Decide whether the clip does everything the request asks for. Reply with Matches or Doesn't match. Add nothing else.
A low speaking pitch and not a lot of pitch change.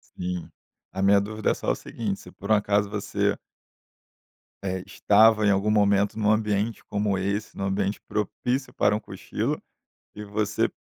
Matches